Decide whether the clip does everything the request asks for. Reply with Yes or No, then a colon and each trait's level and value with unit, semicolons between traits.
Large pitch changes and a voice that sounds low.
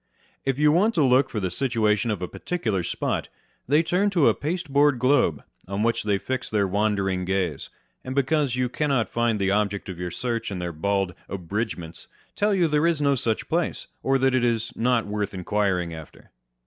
Yes: wide, 6.1 semitones; low, 115 Hz